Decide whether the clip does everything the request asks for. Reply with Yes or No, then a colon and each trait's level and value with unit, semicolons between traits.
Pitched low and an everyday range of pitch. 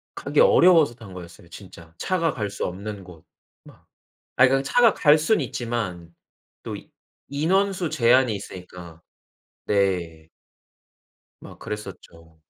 No: low, 105 Hz; wide, 8.7 semitones